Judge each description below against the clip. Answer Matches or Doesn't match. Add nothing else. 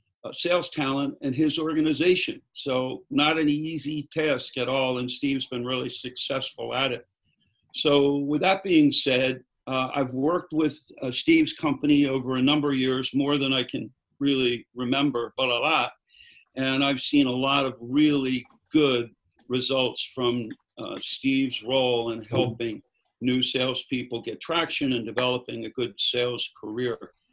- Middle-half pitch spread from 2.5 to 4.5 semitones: Matches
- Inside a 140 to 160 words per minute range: Matches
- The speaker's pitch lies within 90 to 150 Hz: Matches